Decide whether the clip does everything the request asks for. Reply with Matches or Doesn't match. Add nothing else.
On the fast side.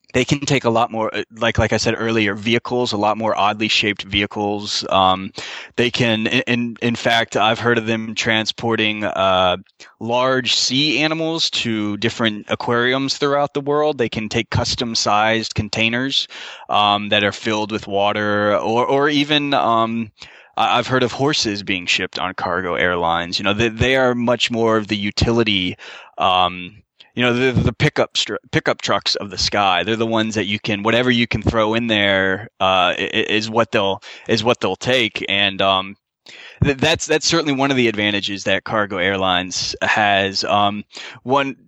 Doesn't match